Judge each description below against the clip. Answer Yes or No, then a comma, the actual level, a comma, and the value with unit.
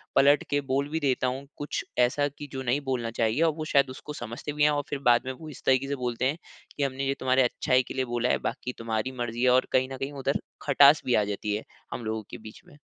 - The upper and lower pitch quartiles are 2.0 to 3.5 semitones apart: Yes, average, 2.8 semitones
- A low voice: Yes, low, 130 Hz